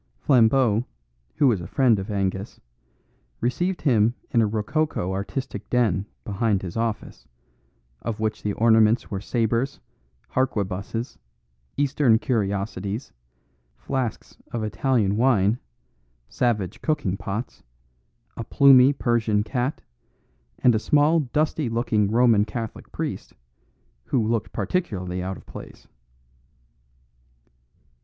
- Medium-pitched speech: No, low, 115 Hz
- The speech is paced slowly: Yes, slow, 110 wpm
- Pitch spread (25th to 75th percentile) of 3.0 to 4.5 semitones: Yes, average, 3.8 semitones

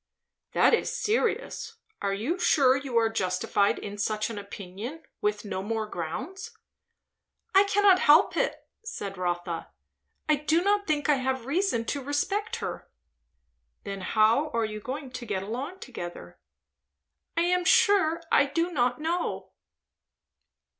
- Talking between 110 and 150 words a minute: Yes, average, 140 wpm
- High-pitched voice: Yes, very high, 270 Hz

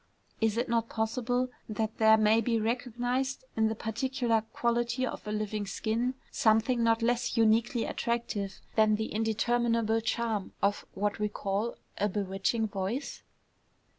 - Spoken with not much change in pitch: Yes, narrow, 1.9 semitones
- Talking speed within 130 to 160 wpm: Yes, average, 140 wpm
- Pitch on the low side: No, high, 225 Hz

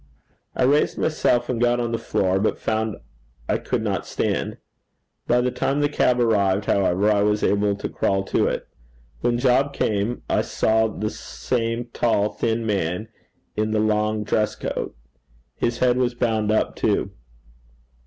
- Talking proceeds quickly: No, average, 165 wpm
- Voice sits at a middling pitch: No, low, 110 Hz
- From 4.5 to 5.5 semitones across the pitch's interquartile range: No, narrow, 2.5 semitones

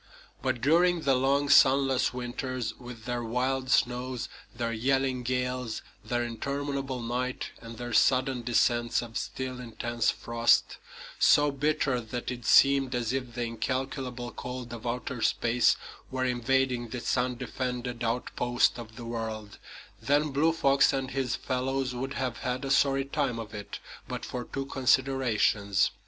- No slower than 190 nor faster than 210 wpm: No, average, 145 wpm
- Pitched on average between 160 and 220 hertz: No, low, 125 Hz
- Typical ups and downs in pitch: No, narrow, 2.0 semitones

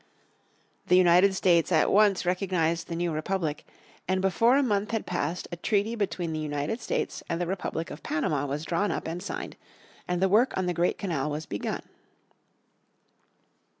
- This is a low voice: No, medium, 180 Hz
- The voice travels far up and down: No, average, 3.4 semitones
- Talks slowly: No, average, 175 wpm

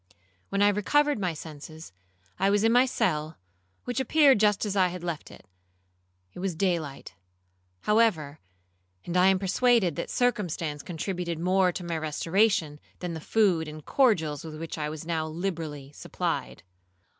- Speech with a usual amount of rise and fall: Yes, average, 4.6 semitones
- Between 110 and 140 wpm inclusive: No, average, 160 wpm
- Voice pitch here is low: No, medium, 175 Hz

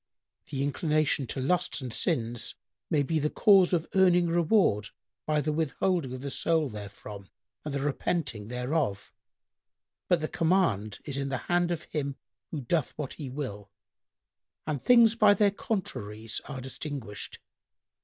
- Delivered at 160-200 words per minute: No, average, 150 wpm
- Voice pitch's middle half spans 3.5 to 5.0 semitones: No, wide, 5.5 semitones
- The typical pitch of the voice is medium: Yes, medium, 145 Hz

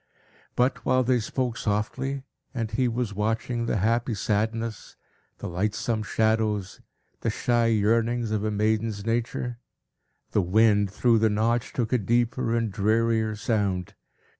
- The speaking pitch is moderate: No, low, 110 Hz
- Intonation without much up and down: Yes, narrow, 1.9 semitones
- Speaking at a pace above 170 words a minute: No, average, 140 wpm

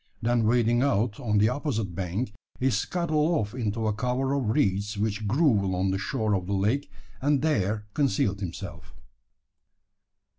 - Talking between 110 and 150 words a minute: No, average, 160 wpm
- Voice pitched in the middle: No, low, 110 Hz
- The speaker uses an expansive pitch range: No, average, 4.8 semitones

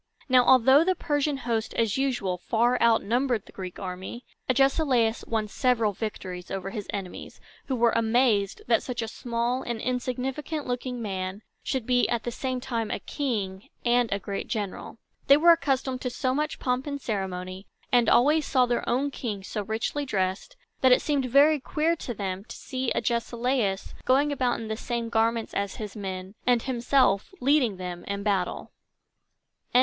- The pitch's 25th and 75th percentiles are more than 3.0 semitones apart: Yes, average, 4.1 semitones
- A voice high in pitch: Yes, high, 235 Hz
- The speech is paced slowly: No, average, 175 wpm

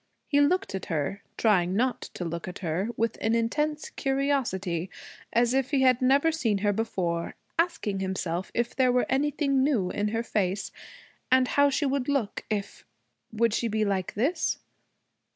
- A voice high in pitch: Yes, high, 230 Hz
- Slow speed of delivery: No, average, 170 wpm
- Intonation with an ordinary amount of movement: No, wide, 5.9 semitones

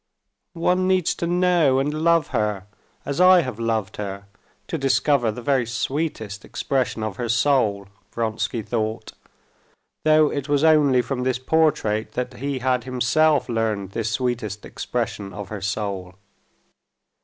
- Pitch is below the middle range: Yes, low, 125 Hz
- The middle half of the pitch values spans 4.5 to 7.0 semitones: Yes, average, 5.3 semitones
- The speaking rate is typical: Yes, average, 145 wpm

